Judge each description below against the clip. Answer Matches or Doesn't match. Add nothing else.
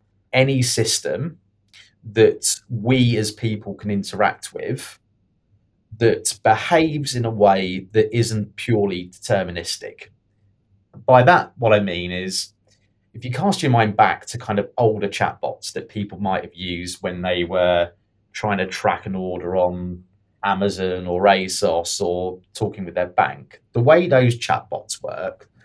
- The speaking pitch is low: Matches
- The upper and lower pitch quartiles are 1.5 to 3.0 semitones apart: Doesn't match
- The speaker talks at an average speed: Matches